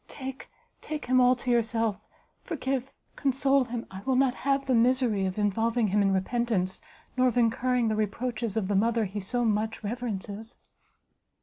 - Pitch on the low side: No, high, 235 Hz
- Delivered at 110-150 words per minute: No, average, 170 wpm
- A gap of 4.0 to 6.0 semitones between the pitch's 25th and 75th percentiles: No, average, 3.3 semitones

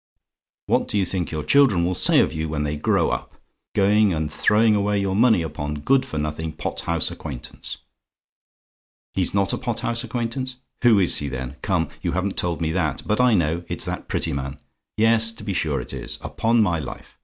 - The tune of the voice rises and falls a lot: Yes, wide, 5.9 semitones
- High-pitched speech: No, very low, 90 Hz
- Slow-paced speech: No, average, 200 wpm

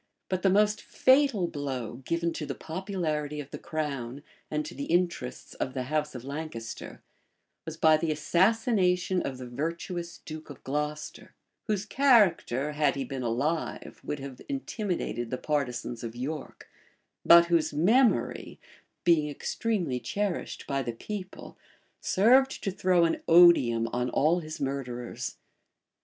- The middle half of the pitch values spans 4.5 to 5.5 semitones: Yes, average, 5.1 semitones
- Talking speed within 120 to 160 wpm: Yes, average, 145 wpm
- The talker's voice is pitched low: No, medium, 155 Hz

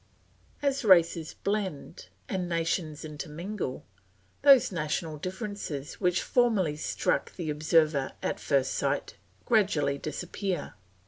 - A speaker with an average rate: No, slow, 105 wpm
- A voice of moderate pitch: Yes, medium, 170 Hz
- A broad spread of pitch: No, average, 4.8 semitones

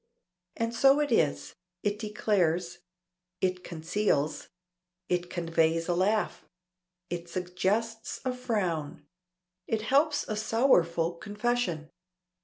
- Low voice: No, medium, 185 Hz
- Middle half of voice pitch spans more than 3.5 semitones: Yes, average, 5.0 semitones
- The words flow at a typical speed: No, slow, 100 wpm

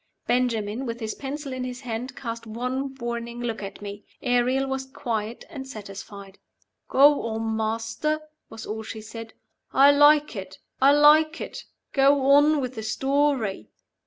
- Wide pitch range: No, average, 3.7 semitones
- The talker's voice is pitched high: Yes, high, 245 Hz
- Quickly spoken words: No, average, 155 wpm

